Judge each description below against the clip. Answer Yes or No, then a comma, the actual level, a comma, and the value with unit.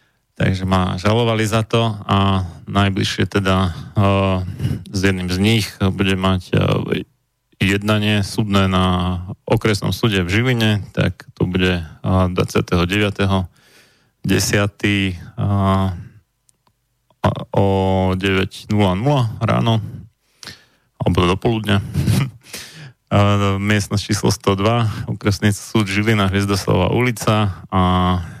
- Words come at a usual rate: No, slow, 95 wpm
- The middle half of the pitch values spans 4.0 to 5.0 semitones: No, average, 3.0 semitones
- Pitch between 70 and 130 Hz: Yes, low, 100 Hz